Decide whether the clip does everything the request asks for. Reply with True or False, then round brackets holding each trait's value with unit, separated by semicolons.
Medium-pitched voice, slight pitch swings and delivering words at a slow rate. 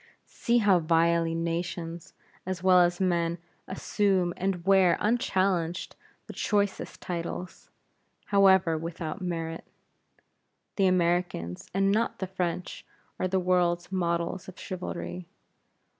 True (180 Hz; 2.0 semitones; 115 wpm)